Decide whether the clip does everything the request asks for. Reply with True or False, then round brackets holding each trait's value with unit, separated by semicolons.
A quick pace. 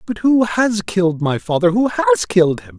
True (215 wpm)